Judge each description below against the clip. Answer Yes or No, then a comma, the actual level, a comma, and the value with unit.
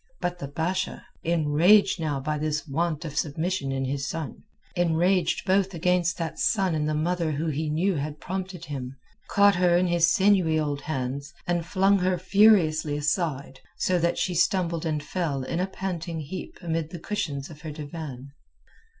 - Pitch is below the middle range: No, medium, 165 Hz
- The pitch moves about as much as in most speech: Yes, average, 3.3 semitones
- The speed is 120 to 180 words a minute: Yes, average, 175 wpm